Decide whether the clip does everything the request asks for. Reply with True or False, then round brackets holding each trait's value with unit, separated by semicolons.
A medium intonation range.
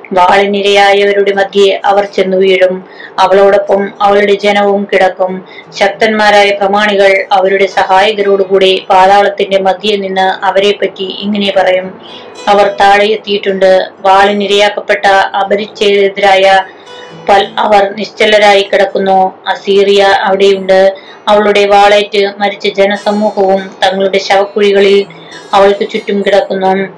False (0.9 semitones)